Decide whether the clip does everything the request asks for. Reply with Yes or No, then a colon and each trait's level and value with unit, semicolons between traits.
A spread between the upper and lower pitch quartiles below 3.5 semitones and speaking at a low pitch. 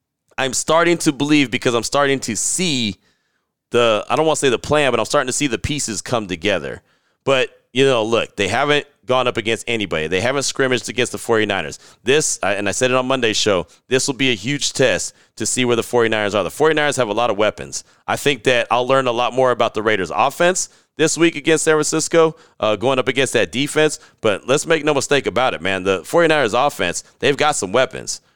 No: average, 4.5 semitones; low, 130 Hz